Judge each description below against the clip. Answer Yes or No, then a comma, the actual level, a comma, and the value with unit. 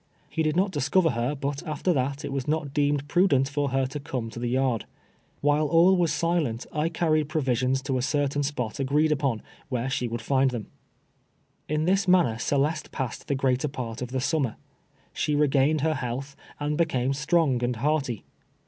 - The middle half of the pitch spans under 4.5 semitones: Yes, average, 3.1 semitones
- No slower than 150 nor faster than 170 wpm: No, average, 185 wpm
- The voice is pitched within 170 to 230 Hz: No, medium, 140 Hz